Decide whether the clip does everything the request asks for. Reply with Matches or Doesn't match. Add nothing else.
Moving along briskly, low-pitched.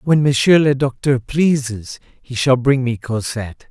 Doesn't match